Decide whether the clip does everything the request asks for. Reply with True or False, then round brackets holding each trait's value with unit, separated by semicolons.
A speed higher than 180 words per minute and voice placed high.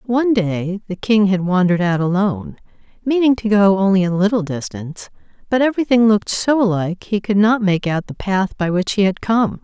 True (200 wpm; 200 Hz)